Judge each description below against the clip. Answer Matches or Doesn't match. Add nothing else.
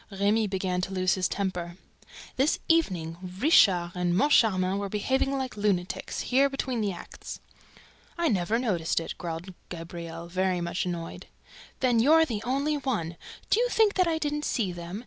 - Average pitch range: Doesn't match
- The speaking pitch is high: Matches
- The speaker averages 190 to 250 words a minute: Doesn't match